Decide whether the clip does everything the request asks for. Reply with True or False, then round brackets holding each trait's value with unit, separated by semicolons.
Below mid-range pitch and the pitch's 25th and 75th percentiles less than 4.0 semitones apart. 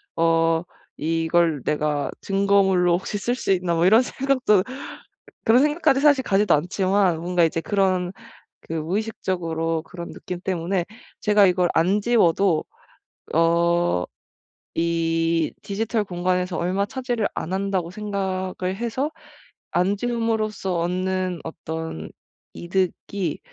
False (185 Hz; 3.4 semitones)